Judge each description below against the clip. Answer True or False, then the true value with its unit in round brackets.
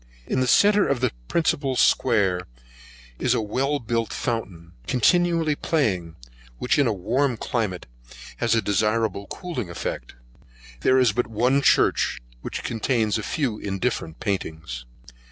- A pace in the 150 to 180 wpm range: False (135 wpm)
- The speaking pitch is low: True (115 Hz)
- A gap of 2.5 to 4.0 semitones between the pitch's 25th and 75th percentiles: False (4.8 semitones)